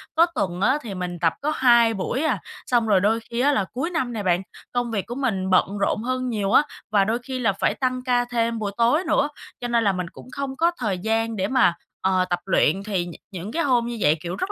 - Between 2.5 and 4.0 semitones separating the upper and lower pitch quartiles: No, average, 4.7 semitones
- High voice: Yes, high, 225 Hz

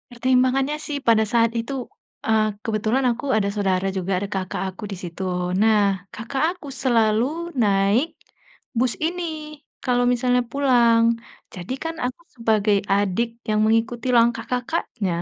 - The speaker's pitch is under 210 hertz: No, high, 230 Hz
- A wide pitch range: No, average, 3.2 semitones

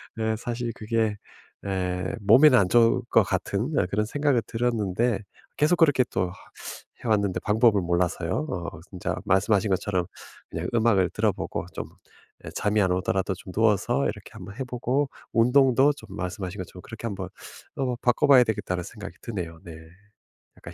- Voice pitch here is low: Yes, low, 105 Hz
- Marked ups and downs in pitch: No, average, 4.5 semitones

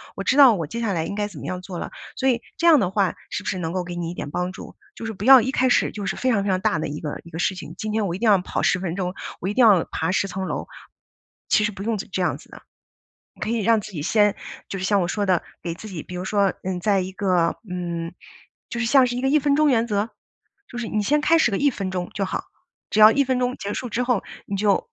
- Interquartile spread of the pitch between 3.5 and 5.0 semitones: Yes, average, 4.1 semitones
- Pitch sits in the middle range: No, high, 200 Hz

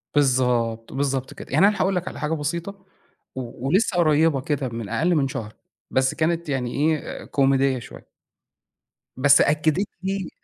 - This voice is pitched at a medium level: Yes, medium, 145 Hz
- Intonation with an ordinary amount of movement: Yes, average, 4.4 semitones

